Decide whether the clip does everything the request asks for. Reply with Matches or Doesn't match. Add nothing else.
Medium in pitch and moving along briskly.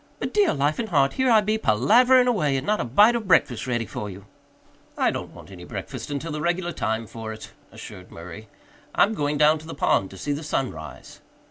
Matches